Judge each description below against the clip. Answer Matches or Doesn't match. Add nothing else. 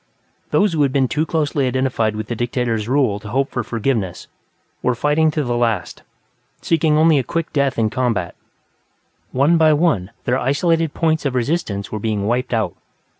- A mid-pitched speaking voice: Doesn't match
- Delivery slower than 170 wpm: Doesn't match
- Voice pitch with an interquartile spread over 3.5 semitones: Matches